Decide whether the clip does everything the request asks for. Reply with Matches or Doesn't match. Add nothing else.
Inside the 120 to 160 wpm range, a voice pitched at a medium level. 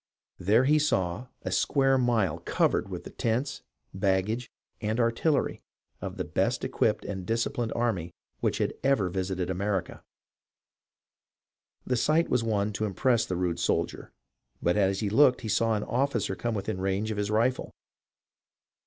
Doesn't match